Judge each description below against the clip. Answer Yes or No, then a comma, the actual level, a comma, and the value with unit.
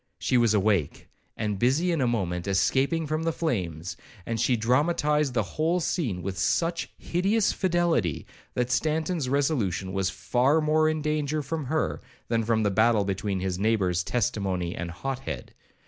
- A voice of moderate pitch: No, low, 125 Hz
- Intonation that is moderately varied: No, wide, 7.9 semitones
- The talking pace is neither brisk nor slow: Yes, average, 160 wpm